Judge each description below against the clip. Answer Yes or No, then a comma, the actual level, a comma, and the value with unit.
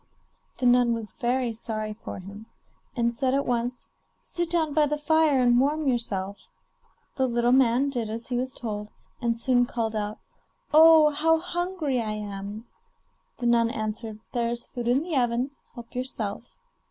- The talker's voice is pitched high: Yes, high, 240 Hz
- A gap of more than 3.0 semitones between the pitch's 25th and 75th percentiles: Yes, average, 3.4 semitones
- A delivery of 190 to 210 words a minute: No, average, 165 wpm